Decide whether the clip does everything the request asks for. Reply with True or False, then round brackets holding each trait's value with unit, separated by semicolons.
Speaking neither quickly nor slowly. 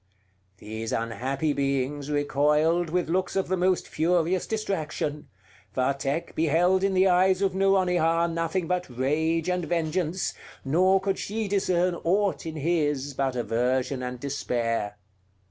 False (130 wpm)